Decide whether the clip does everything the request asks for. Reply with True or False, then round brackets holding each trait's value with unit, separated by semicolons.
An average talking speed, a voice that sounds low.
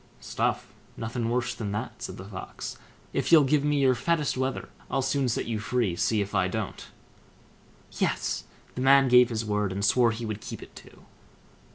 True (190 wpm; 120 Hz)